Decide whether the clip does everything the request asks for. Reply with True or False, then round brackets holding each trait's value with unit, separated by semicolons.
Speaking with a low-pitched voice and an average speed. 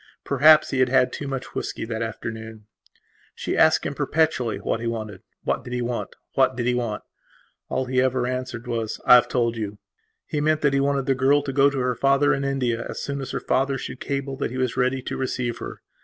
False (130 Hz; 230 wpm)